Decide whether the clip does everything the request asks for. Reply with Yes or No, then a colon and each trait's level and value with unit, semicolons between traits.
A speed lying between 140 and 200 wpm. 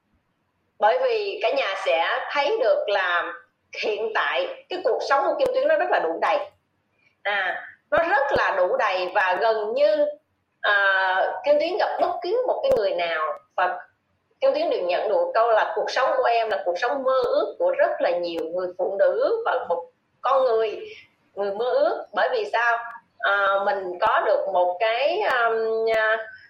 Yes: average, 185 wpm